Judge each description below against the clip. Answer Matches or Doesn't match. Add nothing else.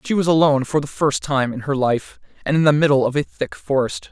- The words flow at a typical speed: Doesn't match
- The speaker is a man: Matches